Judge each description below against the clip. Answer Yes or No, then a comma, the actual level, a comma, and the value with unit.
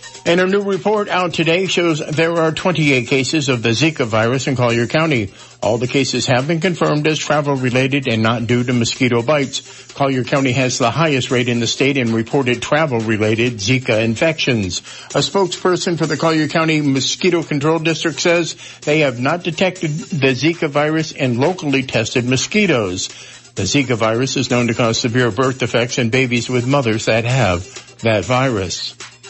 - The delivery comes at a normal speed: Yes, average, 180 wpm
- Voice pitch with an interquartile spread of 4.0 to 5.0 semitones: Yes, average, 4.5 semitones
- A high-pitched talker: No, low, 135 Hz